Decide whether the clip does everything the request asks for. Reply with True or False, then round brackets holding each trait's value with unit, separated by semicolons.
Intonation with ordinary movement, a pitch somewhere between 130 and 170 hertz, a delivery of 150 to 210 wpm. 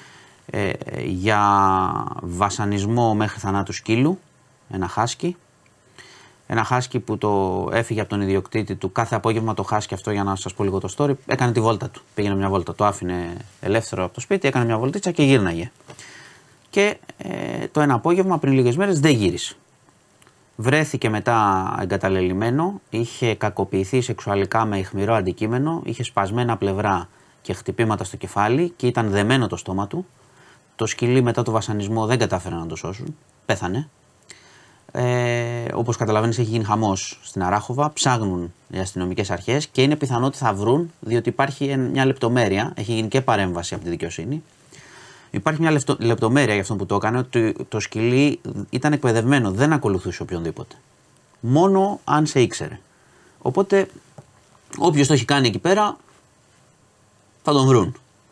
False (5.0 semitones; 115 Hz; 155 wpm)